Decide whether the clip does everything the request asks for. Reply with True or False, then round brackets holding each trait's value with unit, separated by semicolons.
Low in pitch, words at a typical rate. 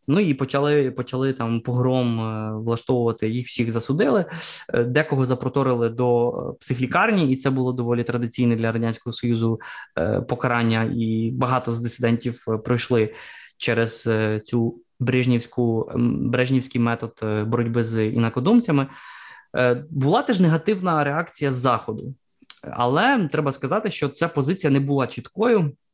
True (125 Hz; 120 wpm)